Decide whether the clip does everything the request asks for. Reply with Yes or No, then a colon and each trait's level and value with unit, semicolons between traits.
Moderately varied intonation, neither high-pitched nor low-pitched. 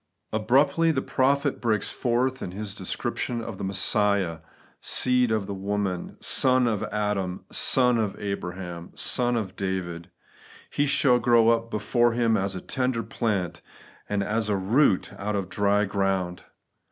No: average, 3.8 semitones; low, 105 Hz